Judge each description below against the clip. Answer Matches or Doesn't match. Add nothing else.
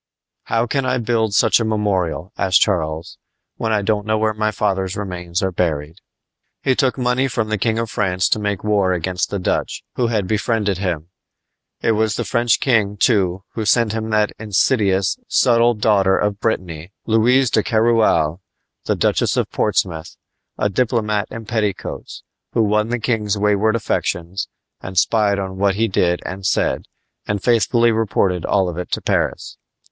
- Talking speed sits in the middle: Matches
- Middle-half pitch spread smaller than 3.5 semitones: Matches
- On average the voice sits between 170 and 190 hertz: Doesn't match